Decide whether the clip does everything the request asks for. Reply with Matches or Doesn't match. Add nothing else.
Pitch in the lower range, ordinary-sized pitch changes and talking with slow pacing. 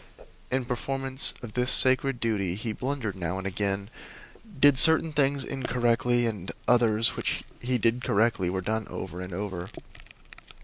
Doesn't match